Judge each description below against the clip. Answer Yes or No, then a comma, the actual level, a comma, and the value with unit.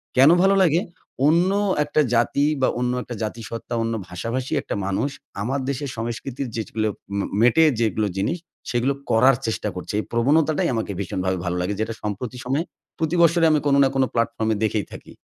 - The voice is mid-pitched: No, low, 120 Hz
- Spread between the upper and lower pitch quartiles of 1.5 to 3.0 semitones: No, average, 4.5 semitones